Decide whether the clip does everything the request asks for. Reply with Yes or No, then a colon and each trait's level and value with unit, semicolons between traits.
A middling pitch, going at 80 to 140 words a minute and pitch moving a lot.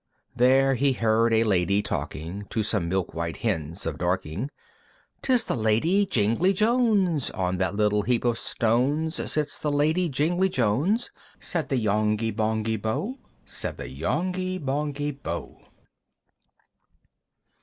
No: low, 120 Hz; slow, 135 wpm; wide, 7.0 semitones